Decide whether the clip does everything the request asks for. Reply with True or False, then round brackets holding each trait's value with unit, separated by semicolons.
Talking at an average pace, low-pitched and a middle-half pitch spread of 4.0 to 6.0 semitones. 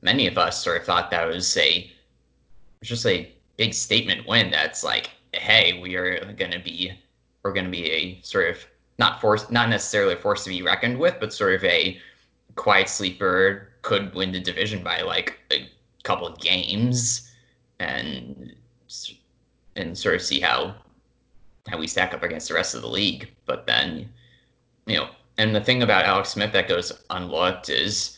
True (180 wpm; 105 Hz; 4.7 semitones)